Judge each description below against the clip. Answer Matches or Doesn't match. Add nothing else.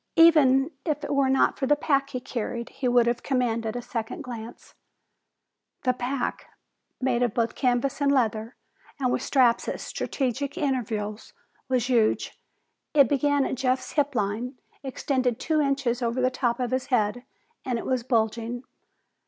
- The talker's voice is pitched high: Matches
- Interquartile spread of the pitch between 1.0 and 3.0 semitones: Matches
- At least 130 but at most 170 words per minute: Matches